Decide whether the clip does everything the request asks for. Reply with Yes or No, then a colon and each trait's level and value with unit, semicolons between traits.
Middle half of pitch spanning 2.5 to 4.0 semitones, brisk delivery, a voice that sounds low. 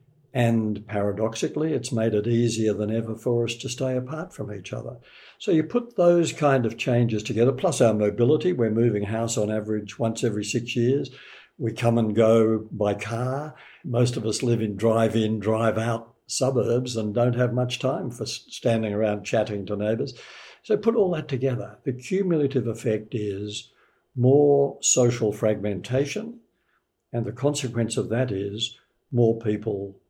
No: average, 3.2 semitones; average, 165 wpm; low, 115 Hz